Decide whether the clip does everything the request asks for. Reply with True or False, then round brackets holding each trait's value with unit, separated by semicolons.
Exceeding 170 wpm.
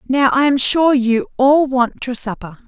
True (200 wpm)